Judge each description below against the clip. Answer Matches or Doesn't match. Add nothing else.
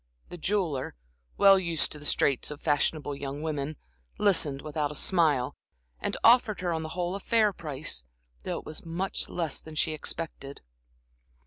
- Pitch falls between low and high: Matches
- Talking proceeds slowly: Doesn't match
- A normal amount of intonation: Matches